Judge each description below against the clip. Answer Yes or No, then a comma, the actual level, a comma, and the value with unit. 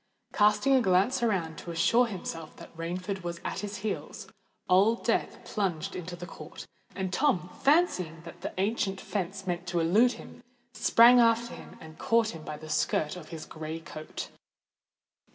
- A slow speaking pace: No, average, 170 wpm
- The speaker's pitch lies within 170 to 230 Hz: Yes, medium, 185 Hz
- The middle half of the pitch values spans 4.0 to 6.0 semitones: Yes, average, 4.9 semitones